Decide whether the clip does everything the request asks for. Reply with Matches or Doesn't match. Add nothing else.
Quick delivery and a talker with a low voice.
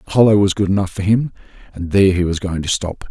Matches